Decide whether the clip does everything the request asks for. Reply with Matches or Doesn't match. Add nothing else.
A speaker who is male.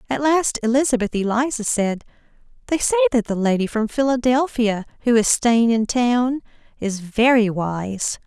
Doesn't match